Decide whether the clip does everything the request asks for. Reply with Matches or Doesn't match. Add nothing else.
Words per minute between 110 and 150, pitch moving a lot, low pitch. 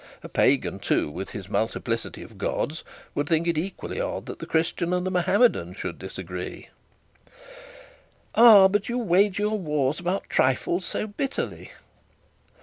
Doesn't match